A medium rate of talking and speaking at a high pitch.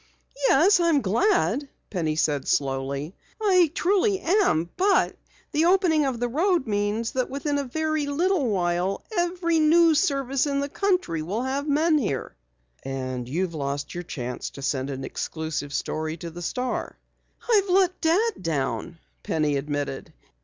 Yes: average, 150 wpm; very high, 255 Hz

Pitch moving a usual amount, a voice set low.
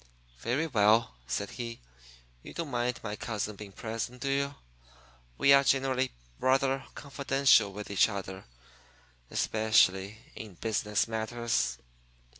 Yes: average, 4.2 semitones; low, 115 Hz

